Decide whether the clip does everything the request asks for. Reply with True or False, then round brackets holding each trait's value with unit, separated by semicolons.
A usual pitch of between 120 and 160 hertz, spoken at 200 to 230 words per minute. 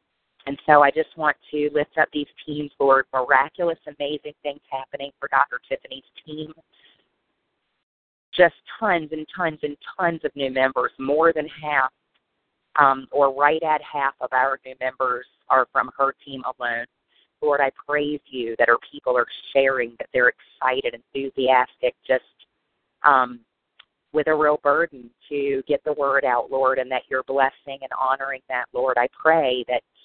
False (140 Hz; 160 wpm)